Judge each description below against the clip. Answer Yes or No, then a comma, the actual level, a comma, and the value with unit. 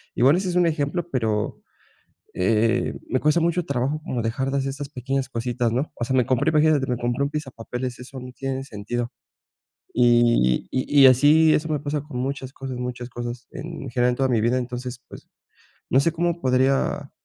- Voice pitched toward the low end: Yes, low, 130 Hz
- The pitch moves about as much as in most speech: Yes, average, 3.1 semitones